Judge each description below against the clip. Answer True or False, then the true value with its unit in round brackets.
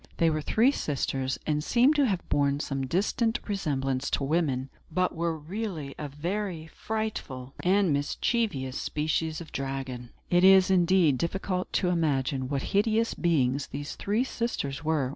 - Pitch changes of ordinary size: False (5.8 semitones)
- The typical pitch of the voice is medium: True (160 Hz)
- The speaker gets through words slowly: False (150 wpm)